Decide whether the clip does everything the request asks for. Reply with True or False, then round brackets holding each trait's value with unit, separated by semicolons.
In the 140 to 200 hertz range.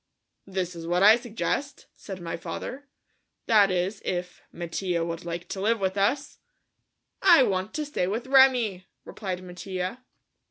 True (190 Hz)